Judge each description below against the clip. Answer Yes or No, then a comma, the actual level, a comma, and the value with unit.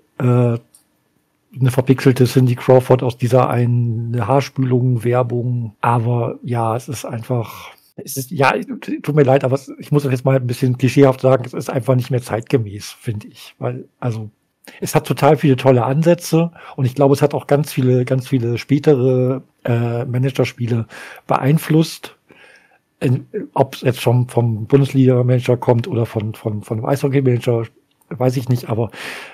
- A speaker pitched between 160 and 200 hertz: No, low, 130 Hz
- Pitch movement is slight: Yes, narrow, 2.3 semitones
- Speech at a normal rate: Yes, average, 160 wpm